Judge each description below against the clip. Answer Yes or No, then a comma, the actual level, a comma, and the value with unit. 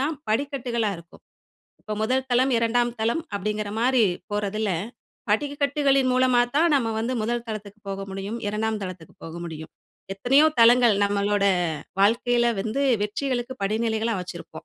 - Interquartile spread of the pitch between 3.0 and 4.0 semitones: Yes, average, 3.7 semitones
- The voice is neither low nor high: No, high, 225 Hz